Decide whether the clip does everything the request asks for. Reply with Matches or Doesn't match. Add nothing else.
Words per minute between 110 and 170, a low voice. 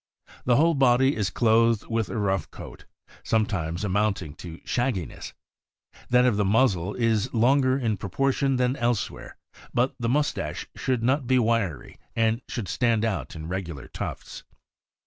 Matches